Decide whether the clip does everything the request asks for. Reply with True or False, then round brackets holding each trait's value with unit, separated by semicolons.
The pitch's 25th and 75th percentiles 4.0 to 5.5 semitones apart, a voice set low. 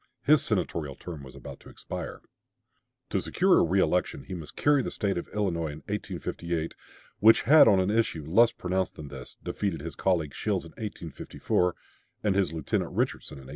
True (4.5 semitones; 90 Hz)